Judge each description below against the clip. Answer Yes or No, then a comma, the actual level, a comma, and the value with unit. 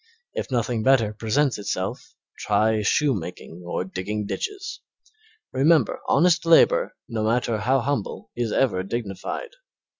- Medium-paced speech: No, slow, 120 wpm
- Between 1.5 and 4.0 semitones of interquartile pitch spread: No, average, 5.0 semitones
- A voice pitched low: Yes, low, 115 Hz